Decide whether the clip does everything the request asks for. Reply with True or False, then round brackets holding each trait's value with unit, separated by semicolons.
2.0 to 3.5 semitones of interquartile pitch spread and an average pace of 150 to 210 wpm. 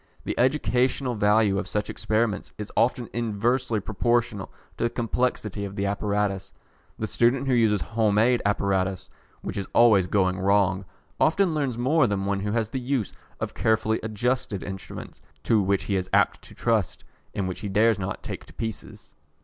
True (3.2 semitones; 175 wpm)